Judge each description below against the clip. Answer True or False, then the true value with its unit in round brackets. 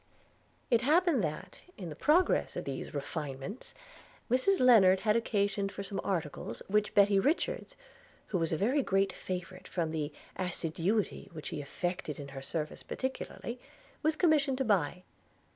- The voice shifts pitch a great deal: True (7.0 semitones)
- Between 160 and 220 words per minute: False (150 wpm)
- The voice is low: False (195 Hz)